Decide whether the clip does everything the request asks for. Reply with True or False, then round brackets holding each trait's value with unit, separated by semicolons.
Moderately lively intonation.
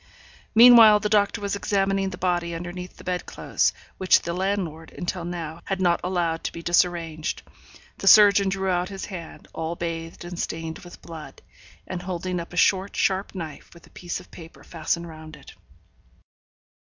False (2.3 semitones)